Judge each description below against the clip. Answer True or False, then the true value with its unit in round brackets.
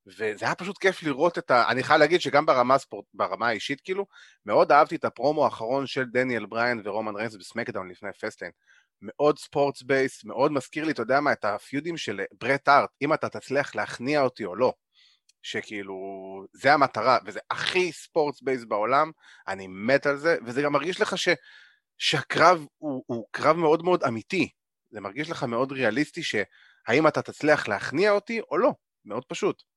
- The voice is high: False (140 Hz)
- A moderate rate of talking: False (175 wpm)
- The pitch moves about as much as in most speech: True (4.9 semitones)